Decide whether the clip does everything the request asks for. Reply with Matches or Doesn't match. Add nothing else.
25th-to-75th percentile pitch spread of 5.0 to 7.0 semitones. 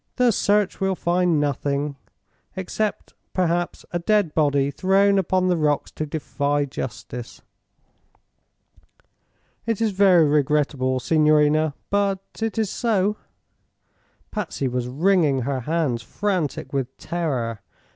Matches